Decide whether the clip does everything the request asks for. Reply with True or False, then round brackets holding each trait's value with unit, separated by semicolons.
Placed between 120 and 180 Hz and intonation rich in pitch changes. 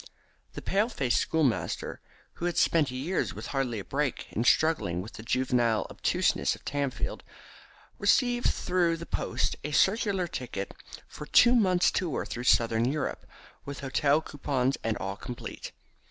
True (140 Hz; 5.8 semitones)